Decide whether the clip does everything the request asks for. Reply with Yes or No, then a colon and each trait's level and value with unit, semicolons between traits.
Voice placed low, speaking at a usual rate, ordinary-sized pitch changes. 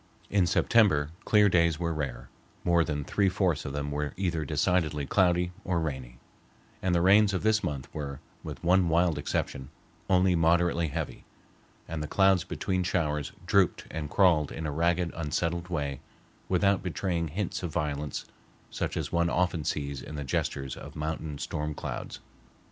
Yes: very low, 85 Hz; average, 165 wpm; average, 3.4 semitones